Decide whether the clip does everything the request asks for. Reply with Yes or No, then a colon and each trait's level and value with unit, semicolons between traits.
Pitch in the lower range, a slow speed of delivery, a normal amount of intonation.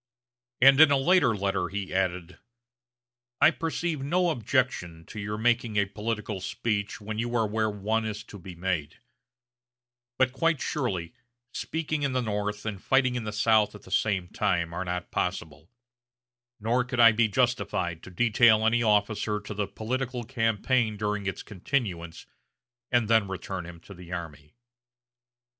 No: low, 105 Hz; average, 160 wpm; average, 4.2 semitones